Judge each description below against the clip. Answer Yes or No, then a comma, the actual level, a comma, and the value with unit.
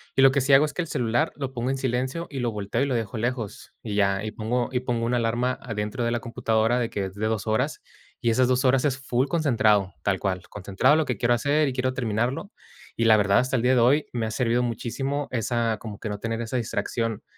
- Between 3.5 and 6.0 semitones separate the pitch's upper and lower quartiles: No, average, 2.9 semitones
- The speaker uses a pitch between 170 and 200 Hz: No, low, 120 Hz